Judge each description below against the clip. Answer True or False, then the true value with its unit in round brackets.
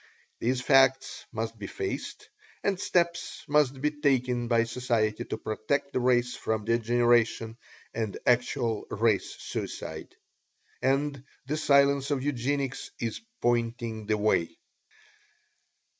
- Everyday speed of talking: False (115 wpm)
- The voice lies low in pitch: True (125 Hz)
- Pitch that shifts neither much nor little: True (3.5 semitones)